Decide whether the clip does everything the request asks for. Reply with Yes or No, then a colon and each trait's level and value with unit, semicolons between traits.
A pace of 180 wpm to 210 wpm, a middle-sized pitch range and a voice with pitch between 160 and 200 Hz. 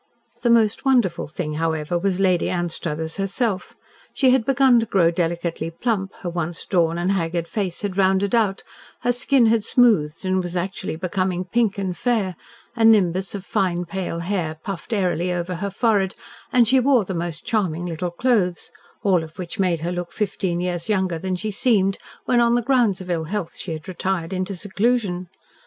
Yes: average, 185 wpm; average, 3.7 semitones; medium, 185 Hz